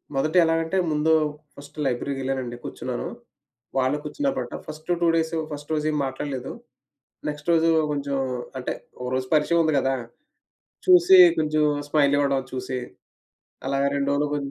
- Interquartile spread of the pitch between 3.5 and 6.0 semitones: No, average, 2.8 semitones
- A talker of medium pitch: Yes, medium, 145 Hz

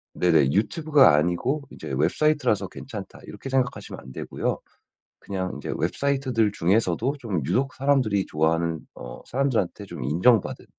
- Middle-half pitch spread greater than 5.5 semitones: Yes, wide, 8.2 semitones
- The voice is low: Yes, low, 105 Hz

